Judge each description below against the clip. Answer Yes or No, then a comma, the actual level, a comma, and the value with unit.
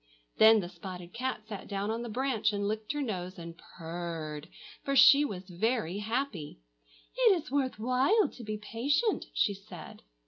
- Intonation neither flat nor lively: No, wide, 6.1 semitones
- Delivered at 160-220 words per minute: Yes, average, 170 wpm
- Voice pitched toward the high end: Yes, high, 215 Hz